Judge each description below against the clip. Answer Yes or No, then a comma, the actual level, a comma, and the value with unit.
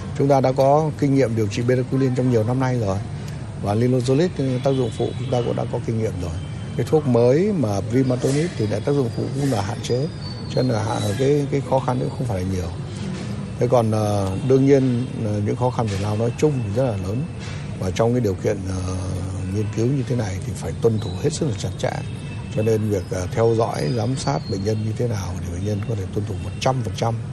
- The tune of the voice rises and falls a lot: No, average, 4.0 semitones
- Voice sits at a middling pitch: No, low, 120 Hz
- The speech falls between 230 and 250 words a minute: Yes, average, 240 wpm